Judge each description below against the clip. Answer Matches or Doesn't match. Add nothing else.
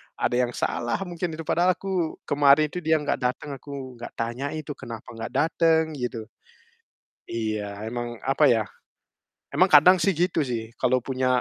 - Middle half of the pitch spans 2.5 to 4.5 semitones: Doesn't match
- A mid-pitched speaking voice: Matches